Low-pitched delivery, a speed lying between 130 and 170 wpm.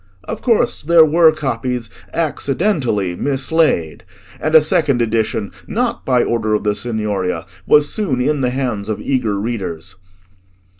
Yes: low, 125 Hz; average, 140 wpm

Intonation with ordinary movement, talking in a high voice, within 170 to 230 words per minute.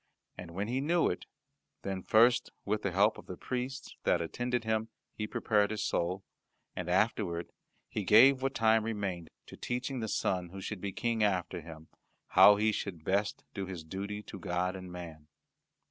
No: average, 3.6 semitones; low, 100 Hz; average, 180 wpm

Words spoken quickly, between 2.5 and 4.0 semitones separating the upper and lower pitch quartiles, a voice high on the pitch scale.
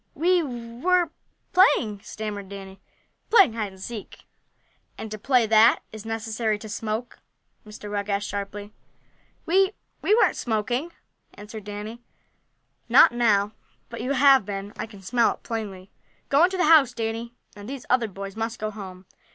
No: average, 160 wpm; average, 3.3 semitones; high, 220 Hz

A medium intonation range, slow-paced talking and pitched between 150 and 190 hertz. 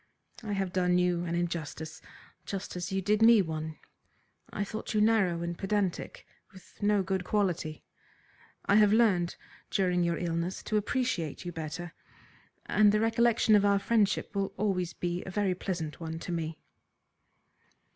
No: average, 3.2 semitones; average, 155 wpm; medium, 185 Hz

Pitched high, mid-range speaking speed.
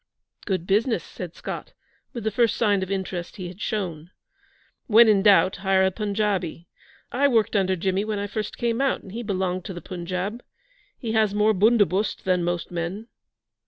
Yes: high, 195 Hz; average, 180 wpm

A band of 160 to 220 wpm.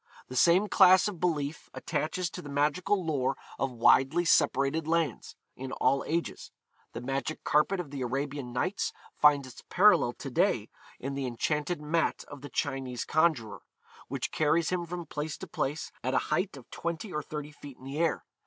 Yes: average, 180 wpm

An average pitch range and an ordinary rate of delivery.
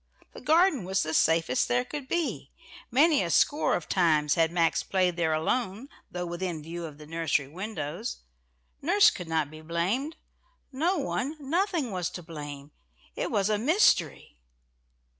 No: wide, 8.8 semitones; average, 160 wpm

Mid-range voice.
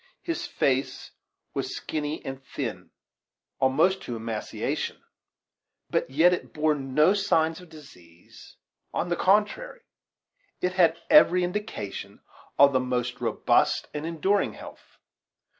Yes: medium, 155 Hz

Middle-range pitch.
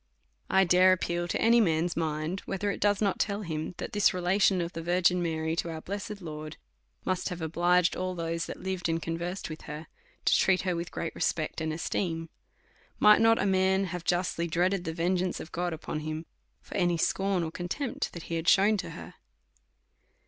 Yes: medium, 175 Hz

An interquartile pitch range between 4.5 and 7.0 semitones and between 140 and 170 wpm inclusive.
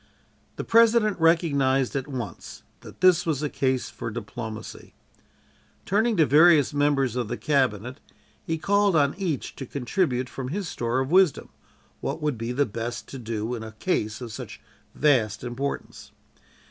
Yes: average, 5.3 semitones; average, 155 wpm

